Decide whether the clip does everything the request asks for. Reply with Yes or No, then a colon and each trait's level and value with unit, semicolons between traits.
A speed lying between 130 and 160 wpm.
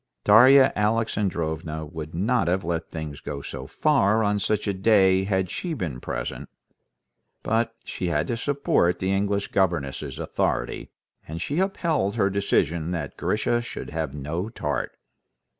Yes: average, 145 wpm